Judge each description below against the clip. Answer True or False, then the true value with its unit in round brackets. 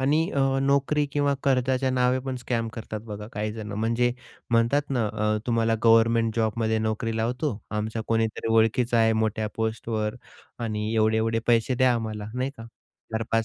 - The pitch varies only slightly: True (2.2 semitones)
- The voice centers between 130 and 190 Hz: False (115 Hz)